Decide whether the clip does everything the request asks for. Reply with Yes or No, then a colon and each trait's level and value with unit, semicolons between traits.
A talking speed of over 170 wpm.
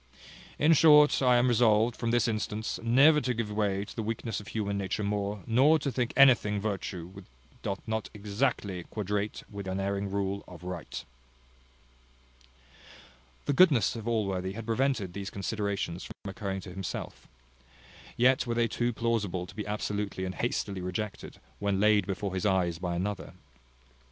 No: average, 160 wpm